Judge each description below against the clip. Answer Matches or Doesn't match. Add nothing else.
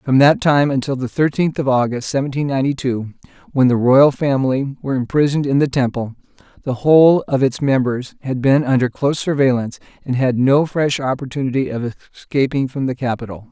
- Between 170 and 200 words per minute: Matches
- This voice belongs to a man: Matches